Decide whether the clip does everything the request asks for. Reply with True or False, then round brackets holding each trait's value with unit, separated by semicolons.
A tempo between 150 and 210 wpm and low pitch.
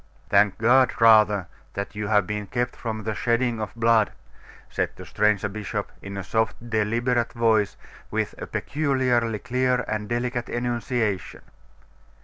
False (140 wpm; 115 Hz)